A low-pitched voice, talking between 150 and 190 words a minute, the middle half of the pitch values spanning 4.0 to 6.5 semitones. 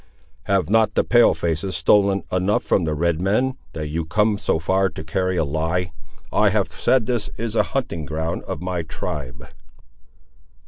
Yes: very low, 90 Hz; average, 180 wpm; average, 4.4 semitones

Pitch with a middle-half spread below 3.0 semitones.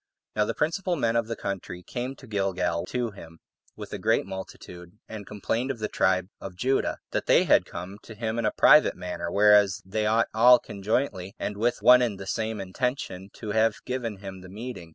No: average, 3.7 semitones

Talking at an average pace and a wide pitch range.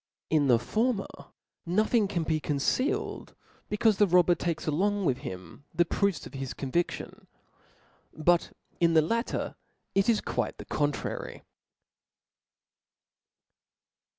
No: slow, 120 wpm; wide, 5.7 semitones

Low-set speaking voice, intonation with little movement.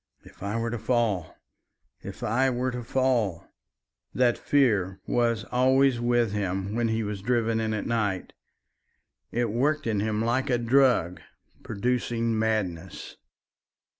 No: low, 115 Hz; average, 3.0 semitones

